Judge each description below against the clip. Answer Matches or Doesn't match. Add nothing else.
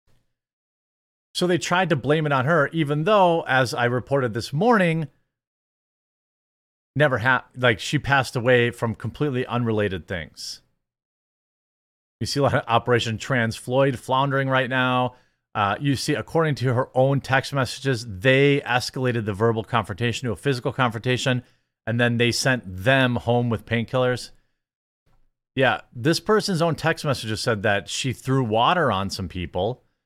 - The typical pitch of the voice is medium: Doesn't match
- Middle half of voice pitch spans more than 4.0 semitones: Doesn't match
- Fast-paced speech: Doesn't match